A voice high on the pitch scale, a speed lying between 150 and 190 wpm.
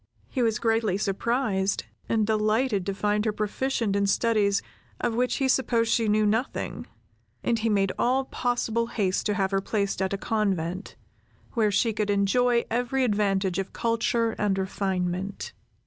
Yes: high, 215 Hz; average, 160 wpm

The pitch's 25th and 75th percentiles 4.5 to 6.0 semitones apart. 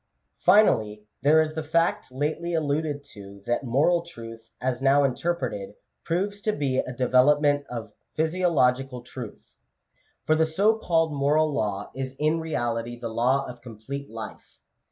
Yes: average, 4.9 semitones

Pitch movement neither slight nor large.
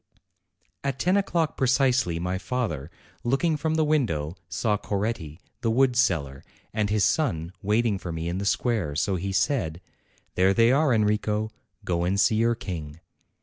No: wide, 6.5 semitones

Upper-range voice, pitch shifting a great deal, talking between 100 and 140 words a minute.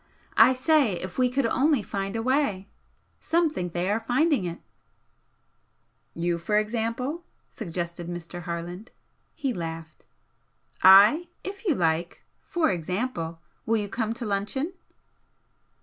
Yes: high, 210 Hz; wide, 6.8 semitones; slow, 135 wpm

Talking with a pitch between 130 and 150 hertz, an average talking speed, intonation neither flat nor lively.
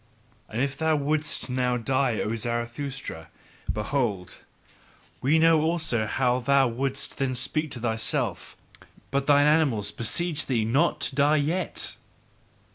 No: low, 135 Hz; slow, 130 wpm; average, 4.1 semitones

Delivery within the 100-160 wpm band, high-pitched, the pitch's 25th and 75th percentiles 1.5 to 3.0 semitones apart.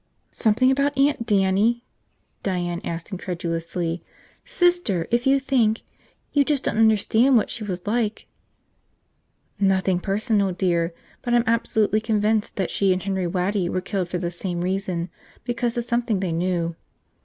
No: average, 150 wpm; high, 200 Hz; average, 4.7 semitones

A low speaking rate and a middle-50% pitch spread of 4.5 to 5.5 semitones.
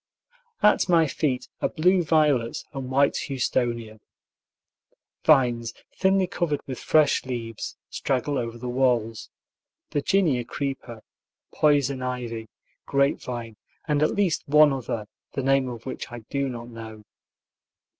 No: slow, 125 wpm; average, 3.9 semitones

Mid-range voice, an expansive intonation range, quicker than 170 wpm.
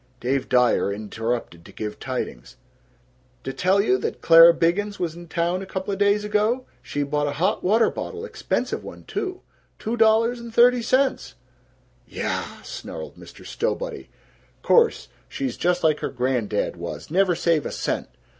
No: medium, 180 Hz; wide, 8.6 semitones; average, 155 wpm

